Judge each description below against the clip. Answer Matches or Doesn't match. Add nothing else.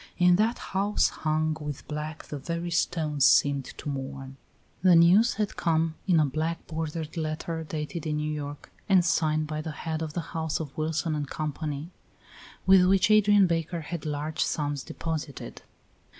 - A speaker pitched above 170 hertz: Doesn't match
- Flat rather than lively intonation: Matches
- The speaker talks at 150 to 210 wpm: Matches